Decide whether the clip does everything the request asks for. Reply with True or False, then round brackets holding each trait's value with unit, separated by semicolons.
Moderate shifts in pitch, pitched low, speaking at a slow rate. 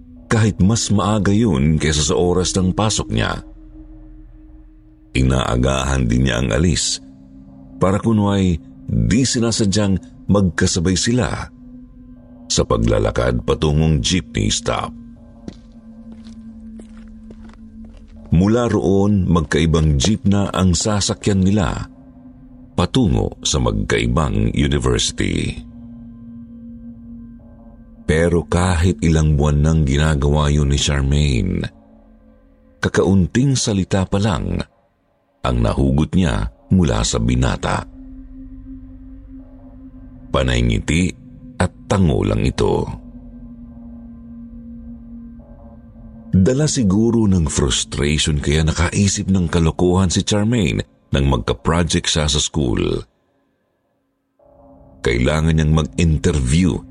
False (7.0 semitones; 95 Hz; 85 wpm)